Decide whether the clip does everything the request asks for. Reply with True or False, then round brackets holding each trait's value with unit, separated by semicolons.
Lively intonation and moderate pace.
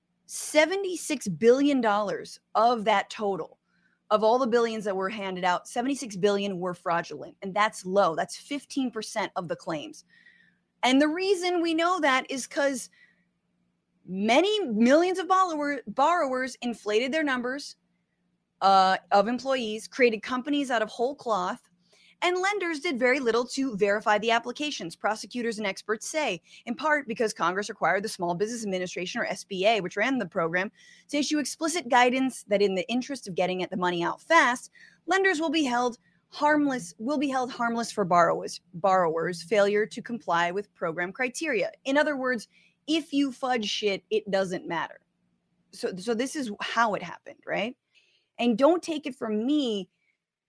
True (6.2 semitones; 160 wpm)